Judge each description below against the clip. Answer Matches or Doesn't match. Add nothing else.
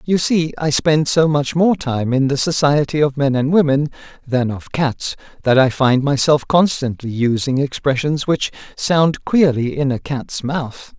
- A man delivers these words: Matches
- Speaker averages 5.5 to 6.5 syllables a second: Doesn't match